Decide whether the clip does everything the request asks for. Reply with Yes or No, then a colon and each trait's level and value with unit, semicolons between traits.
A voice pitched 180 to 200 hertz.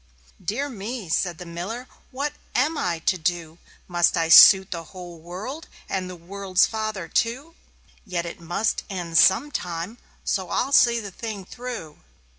Yes: high, 190 Hz